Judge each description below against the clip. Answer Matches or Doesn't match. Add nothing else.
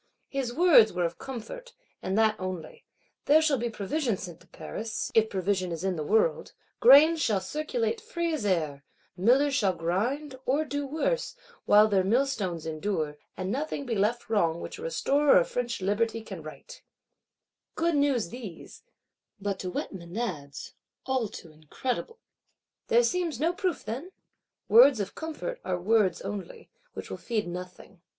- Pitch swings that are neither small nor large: Doesn't match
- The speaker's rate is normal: Matches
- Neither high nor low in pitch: Doesn't match